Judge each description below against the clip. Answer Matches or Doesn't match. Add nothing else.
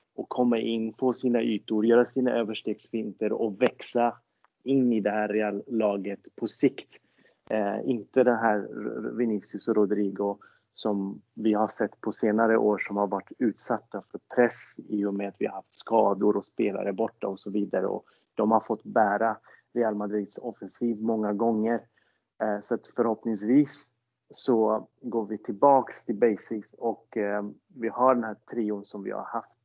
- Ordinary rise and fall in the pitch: Doesn't match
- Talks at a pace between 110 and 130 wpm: Doesn't match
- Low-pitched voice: Matches